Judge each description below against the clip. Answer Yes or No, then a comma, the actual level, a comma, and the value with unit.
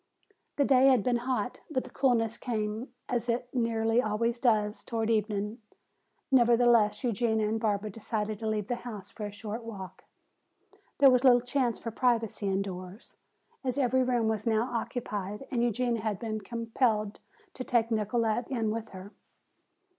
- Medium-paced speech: Yes, average, 160 wpm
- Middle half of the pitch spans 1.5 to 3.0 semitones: Yes, narrow, 2.4 semitones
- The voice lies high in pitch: Yes, high, 230 Hz